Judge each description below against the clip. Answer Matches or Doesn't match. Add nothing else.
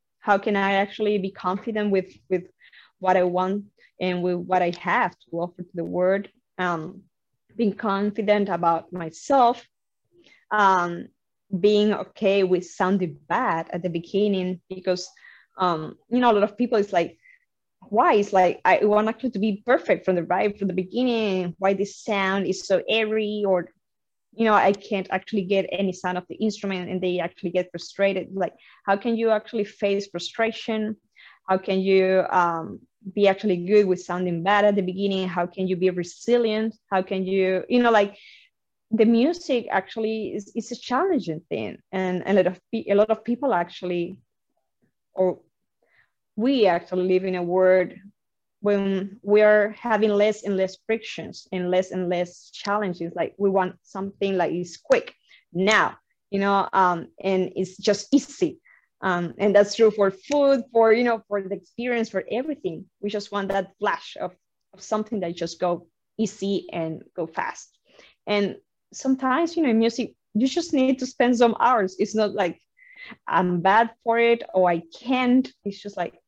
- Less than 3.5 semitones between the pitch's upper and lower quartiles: Matches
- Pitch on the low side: Doesn't match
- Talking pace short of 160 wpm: Doesn't match